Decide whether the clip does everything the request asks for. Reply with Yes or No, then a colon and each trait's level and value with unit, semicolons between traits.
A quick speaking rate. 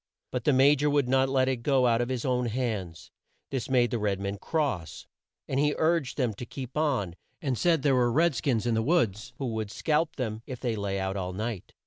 Yes: fast, 235 wpm